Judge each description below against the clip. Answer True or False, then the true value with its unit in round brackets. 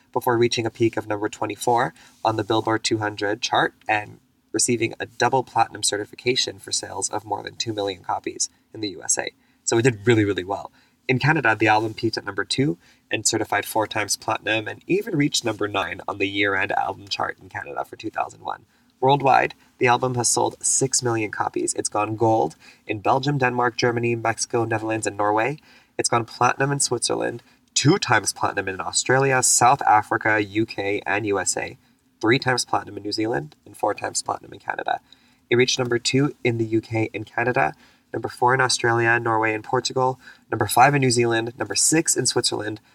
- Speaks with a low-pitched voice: True (115 Hz)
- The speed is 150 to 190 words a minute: True (185 wpm)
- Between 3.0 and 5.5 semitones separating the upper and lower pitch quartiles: False (2.5 semitones)